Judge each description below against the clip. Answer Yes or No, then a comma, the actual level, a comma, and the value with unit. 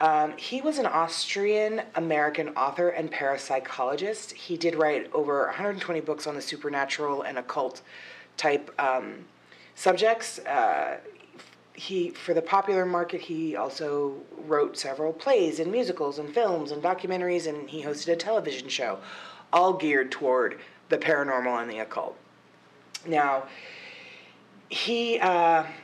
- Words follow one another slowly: Yes, slow, 130 wpm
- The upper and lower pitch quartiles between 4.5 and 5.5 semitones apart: Yes, average, 4.8 semitones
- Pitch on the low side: No, medium, 160 Hz